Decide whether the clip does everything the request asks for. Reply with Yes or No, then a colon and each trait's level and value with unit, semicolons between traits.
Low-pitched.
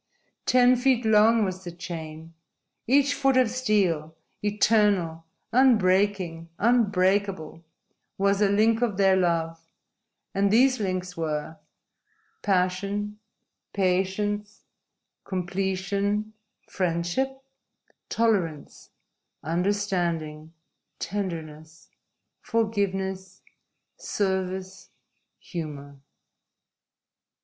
No: high, 190 Hz